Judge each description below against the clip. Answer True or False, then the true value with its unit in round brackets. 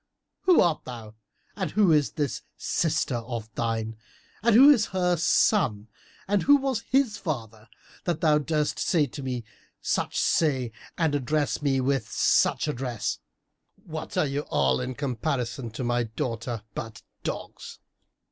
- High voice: False (140 Hz)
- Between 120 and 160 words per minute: True (145 wpm)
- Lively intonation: True (6.1 semitones)